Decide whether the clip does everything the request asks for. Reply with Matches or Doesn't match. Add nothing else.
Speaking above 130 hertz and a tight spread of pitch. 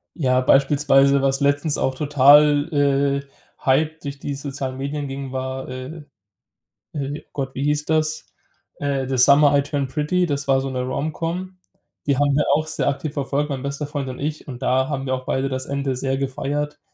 Matches